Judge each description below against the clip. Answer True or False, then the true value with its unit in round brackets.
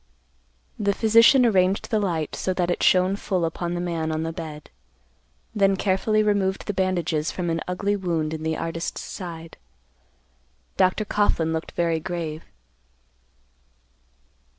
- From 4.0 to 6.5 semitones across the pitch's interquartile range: False (3.3 semitones)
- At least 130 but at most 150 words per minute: True (140 wpm)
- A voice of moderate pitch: True (180 Hz)